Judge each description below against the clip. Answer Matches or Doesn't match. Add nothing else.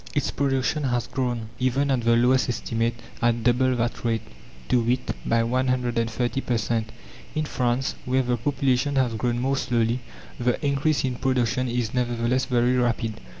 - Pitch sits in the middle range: Doesn't match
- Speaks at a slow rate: Doesn't match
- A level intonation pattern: Matches